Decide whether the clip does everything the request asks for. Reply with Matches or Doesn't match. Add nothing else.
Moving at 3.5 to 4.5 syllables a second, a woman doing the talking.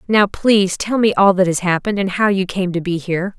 Doesn't match